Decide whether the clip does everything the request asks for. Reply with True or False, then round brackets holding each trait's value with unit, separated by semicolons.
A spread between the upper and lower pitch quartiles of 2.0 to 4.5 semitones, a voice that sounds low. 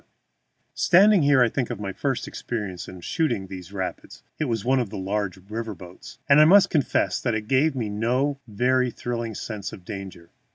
False (5.2 semitones; 115 Hz)